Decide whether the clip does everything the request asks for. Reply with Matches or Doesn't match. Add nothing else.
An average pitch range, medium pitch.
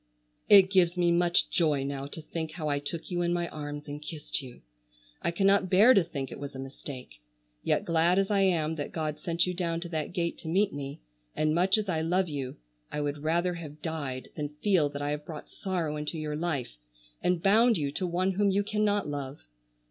Matches